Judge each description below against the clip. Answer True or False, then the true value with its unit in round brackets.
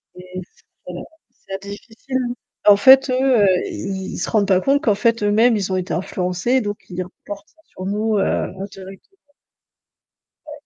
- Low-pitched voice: False (200 Hz)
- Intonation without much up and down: False (3.4 semitones)